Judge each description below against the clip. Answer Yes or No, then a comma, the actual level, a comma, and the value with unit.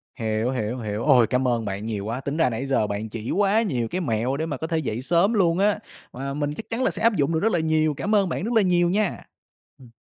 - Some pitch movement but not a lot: No, wide, 7.5 semitones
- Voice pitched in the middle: Yes, medium, 145 Hz